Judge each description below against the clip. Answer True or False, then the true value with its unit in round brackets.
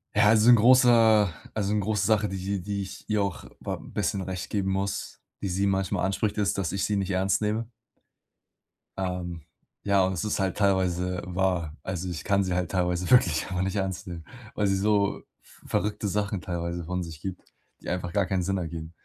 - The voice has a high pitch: False (95 Hz)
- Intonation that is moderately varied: False (2.2 semitones)